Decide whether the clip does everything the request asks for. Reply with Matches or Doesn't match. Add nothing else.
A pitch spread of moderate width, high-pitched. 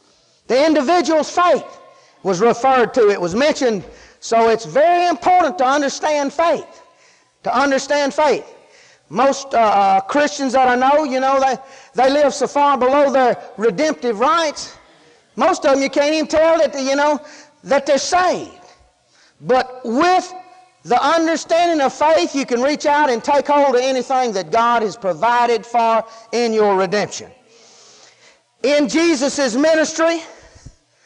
Matches